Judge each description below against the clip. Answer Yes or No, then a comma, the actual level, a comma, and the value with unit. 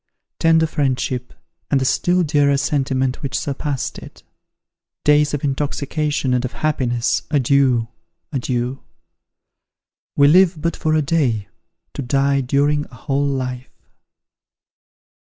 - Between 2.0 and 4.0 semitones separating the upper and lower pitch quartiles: Yes, narrow, 2.4 semitones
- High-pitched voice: No, medium, 140 Hz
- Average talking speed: No, slow, 120 wpm